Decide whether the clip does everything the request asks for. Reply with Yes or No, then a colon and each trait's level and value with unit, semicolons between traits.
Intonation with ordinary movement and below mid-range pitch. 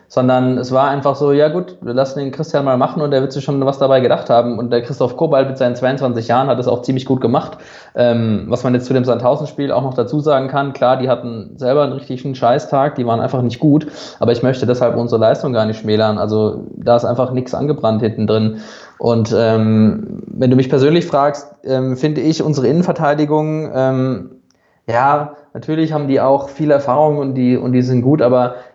Yes: average, 3.0 semitones; low, 130 Hz